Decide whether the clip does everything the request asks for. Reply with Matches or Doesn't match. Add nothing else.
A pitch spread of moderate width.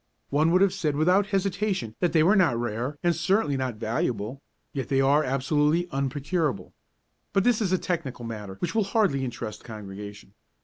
Doesn't match